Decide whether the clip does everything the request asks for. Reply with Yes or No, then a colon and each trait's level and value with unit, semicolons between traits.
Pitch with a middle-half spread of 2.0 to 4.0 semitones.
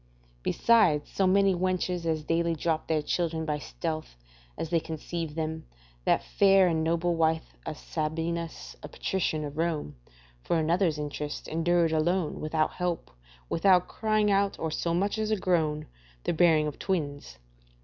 Yes: narrow, 2.4 semitones